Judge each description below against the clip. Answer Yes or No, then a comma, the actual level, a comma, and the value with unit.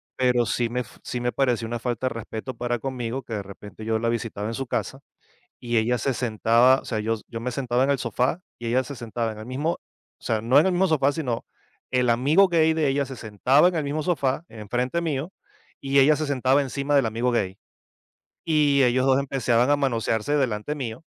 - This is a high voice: No, low, 125 Hz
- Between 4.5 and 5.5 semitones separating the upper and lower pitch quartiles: No, average, 3.2 semitones